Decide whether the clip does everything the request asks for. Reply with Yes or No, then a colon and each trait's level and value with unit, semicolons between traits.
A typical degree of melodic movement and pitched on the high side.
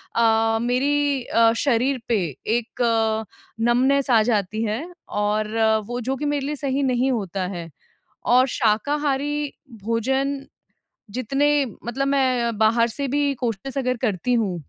Yes: average, 3.6 semitones; high, 245 Hz